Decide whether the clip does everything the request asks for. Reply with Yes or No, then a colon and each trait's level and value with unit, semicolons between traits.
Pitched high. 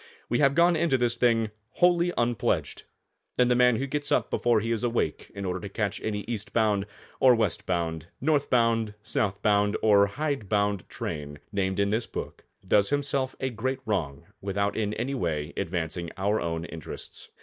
No: low, 110 Hz